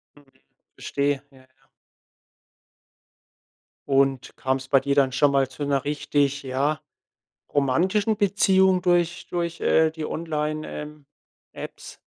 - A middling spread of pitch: Yes, average, 3.6 semitones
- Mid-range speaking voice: Yes, medium, 145 Hz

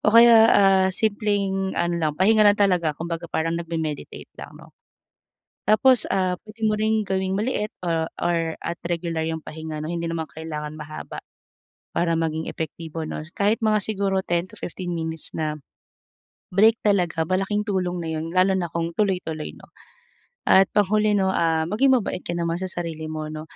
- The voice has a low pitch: No, medium, 175 Hz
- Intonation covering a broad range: No, average, 3.9 semitones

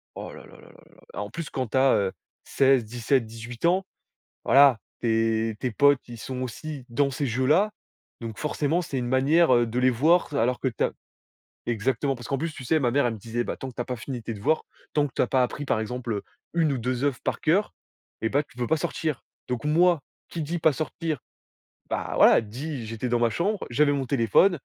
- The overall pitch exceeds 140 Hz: No, low, 130 Hz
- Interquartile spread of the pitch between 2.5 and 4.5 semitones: Yes, average, 4.2 semitones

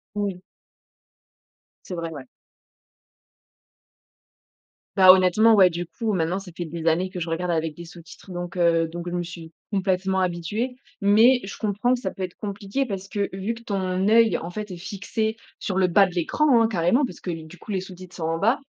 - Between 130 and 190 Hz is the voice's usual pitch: Yes, medium, 185 Hz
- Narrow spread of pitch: No, average, 3.0 semitones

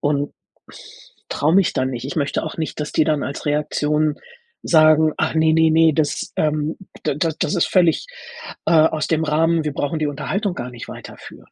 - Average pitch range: No, narrow, 1.5 semitones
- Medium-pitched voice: Yes, medium, 155 Hz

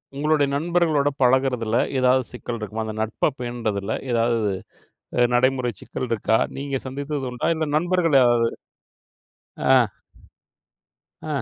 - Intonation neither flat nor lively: Yes, average, 3.5 semitones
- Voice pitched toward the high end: No, low, 130 Hz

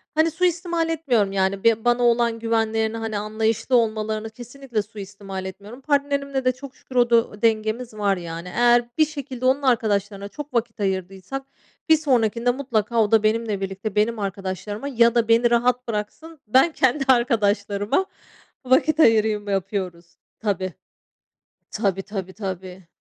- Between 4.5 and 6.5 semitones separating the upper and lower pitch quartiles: No, average, 3.7 semitones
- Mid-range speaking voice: No, high, 225 Hz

